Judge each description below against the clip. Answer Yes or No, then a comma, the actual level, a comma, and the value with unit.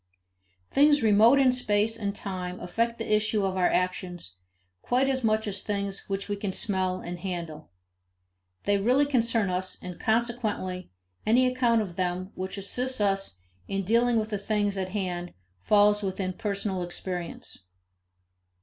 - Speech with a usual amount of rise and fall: Yes, average, 3.4 semitones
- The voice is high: Yes, high, 200 Hz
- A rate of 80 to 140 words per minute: No, average, 150 wpm